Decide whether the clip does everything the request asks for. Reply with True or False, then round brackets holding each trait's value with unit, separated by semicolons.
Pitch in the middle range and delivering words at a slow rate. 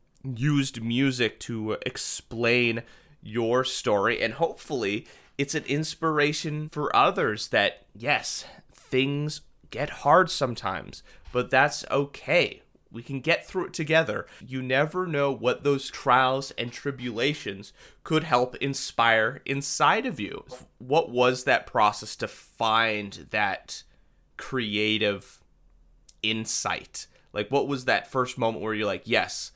False (130 Hz; 125 wpm)